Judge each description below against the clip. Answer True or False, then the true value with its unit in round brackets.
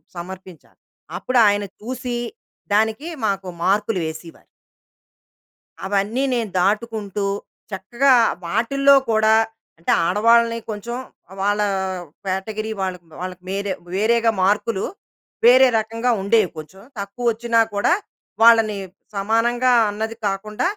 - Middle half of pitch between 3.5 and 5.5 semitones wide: False (3.0 semitones)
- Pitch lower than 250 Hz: True (215 Hz)